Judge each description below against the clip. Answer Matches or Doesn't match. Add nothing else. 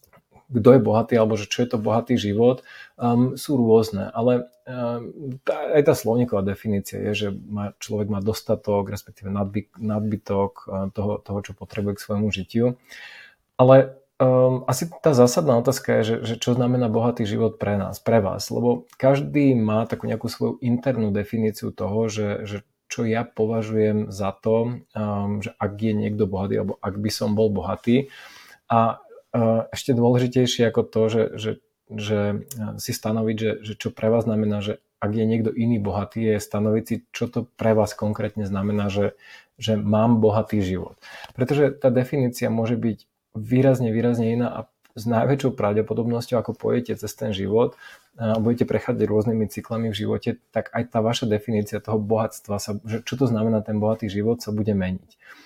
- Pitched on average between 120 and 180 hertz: Doesn't match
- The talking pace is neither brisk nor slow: Doesn't match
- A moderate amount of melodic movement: Doesn't match